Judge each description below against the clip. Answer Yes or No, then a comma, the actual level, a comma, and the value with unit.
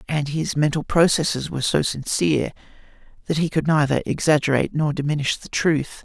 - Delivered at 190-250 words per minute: No, average, 160 wpm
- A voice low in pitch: No, medium, 150 Hz